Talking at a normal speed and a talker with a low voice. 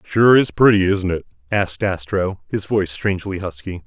Yes: average, 170 wpm; very low, 95 Hz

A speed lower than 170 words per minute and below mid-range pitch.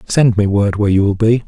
No: fast, 285 wpm; low, 105 Hz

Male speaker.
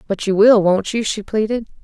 No: female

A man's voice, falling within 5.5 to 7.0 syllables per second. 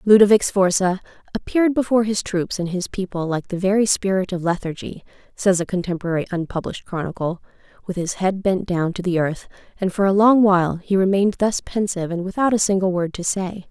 No: female; 5.9 syllables/s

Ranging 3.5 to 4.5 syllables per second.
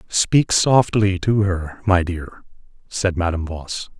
Yes: 3.7 syllables/s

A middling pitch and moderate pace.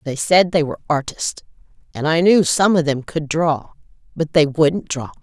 Yes: medium, 155 Hz; average, 185 wpm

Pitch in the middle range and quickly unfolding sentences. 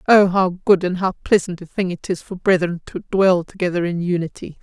Yes: medium, 180 Hz; fast, 220 wpm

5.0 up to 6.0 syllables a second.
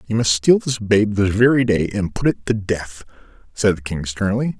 No: 4.8 syllables/s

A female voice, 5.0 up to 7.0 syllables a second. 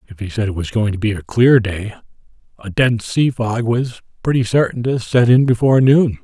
No: male; 5.4 syllables/s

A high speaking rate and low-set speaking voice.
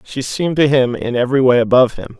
Yes: fast, 245 wpm; low, 130 Hz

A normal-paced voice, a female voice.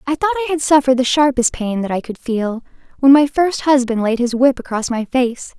No: fast, 235 wpm; female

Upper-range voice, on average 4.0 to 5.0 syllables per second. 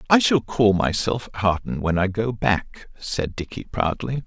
No: low, 105 Hz; 4.2 syllables/s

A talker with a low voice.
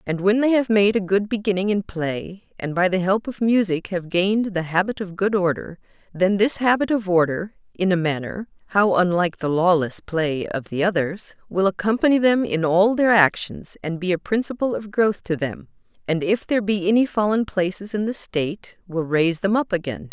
No: high, 190 Hz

